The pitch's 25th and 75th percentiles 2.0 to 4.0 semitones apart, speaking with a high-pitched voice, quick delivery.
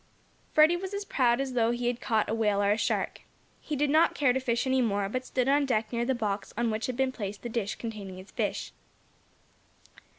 Yes: average, 3.5 semitones; high, 240 Hz; fast, 230 wpm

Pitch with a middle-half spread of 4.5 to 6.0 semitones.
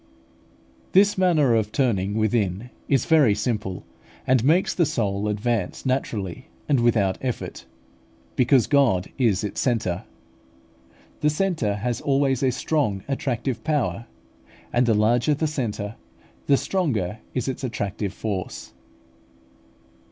Yes: average, 4.9 semitones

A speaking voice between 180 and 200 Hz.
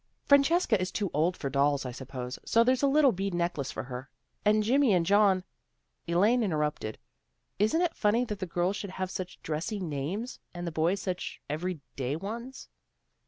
Yes: medium, 185 Hz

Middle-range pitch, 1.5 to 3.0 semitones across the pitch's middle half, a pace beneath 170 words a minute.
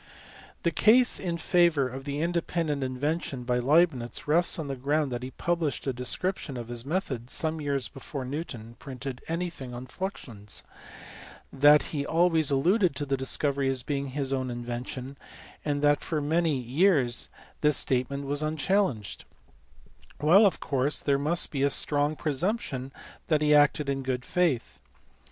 No: medium, 145 Hz; average, 3.7 semitones; average, 160 wpm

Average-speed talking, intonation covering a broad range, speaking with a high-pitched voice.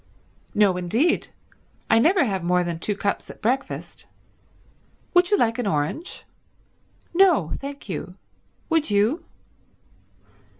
No: slow, 120 wpm; wide, 9.0 semitones; high, 225 Hz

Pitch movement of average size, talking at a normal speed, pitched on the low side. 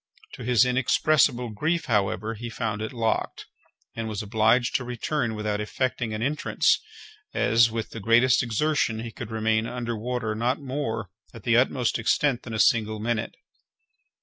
No: narrow, 2.2 semitones; average, 160 wpm; low, 115 Hz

